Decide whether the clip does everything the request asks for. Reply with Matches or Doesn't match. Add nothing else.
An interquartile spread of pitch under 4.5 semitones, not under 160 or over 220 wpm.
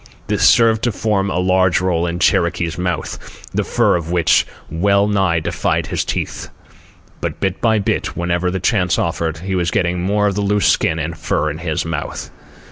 Matches